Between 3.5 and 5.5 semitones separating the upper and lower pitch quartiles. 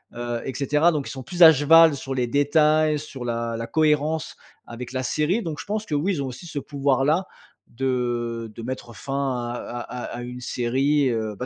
Yes: average, 3.9 semitones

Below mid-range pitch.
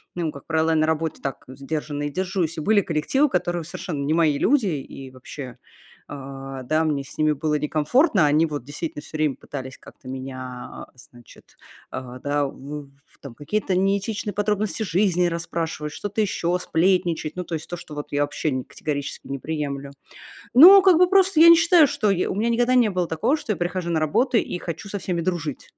No: medium, 160 Hz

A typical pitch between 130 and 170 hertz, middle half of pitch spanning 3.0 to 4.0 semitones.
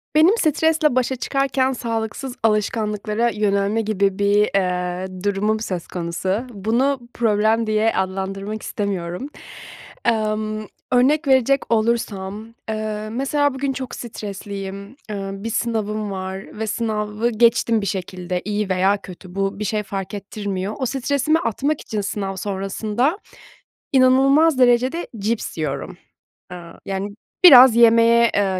No: high, 215 Hz; average, 3.6 semitones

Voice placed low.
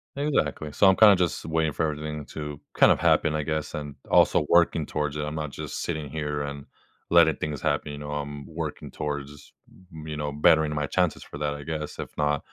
Yes: very low, 75 Hz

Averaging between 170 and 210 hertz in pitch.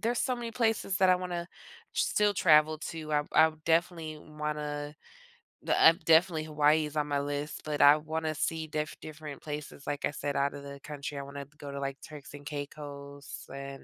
No: medium, 150 Hz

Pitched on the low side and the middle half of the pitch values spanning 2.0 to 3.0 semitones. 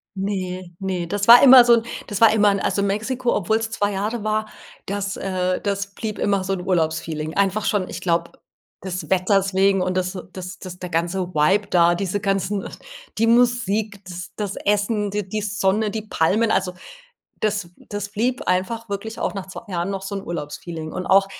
No: high, 195 Hz; narrow, 2.4 semitones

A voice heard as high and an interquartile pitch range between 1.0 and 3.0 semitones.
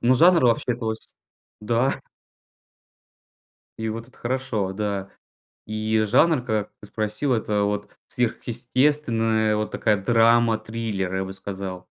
No: low, 110 Hz; narrow, 2.5 semitones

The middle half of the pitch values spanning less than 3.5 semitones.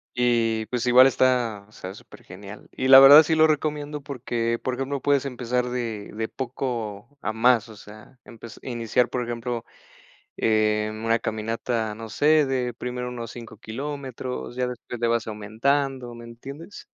Yes: average, 2.8 semitones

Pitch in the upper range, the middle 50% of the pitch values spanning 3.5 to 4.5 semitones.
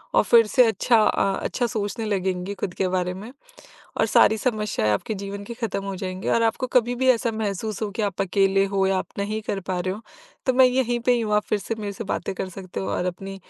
No: high, 200 Hz; average, 2.9 semitones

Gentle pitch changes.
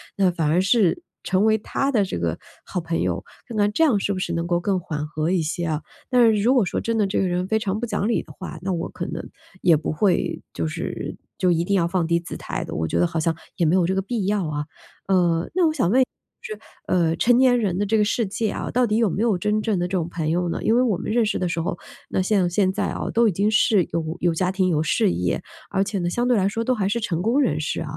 No: average, 4.2 semitones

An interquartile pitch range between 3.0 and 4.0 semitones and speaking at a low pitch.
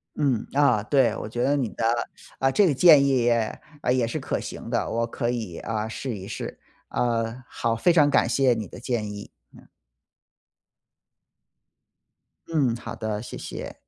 Yes: average, 3.3 semitones; low, 120 Hz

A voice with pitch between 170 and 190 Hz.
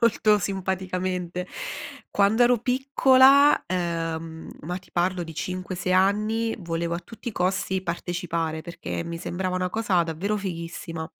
Yes: medium, 185 Hz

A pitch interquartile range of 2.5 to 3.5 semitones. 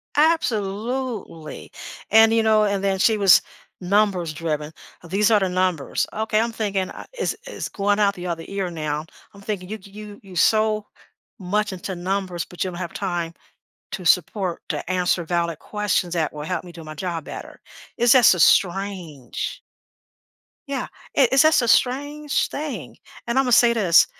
No: average, 3.9 semitones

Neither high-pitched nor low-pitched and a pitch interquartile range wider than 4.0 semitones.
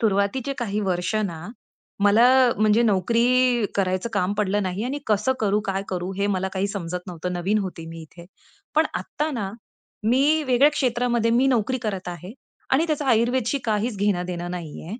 No: high, 210 Hz; average, 4.7 semitones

